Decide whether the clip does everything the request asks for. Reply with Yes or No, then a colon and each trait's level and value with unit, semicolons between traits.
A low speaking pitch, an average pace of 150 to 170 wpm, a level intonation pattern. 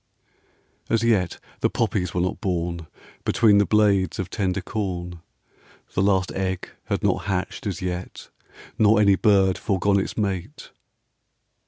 No: very low, 95 Hz; average, 140 wpm; narrow, 2.2 semitones